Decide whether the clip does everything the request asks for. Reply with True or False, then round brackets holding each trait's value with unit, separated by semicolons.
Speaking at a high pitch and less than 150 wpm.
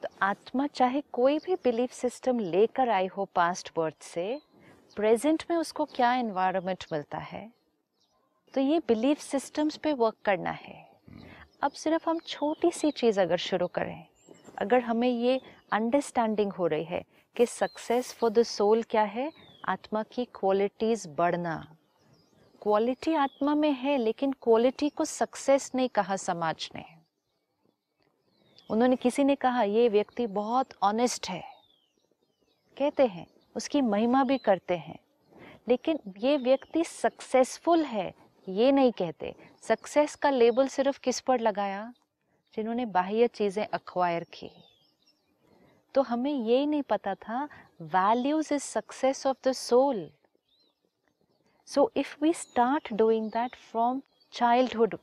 True (240 Hz; 135 wpm)